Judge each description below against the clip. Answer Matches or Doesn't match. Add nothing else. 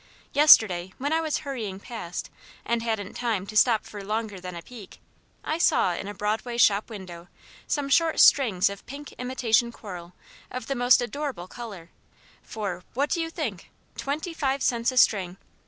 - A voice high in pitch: Matches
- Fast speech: Doesn't match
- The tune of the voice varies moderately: Doesn't match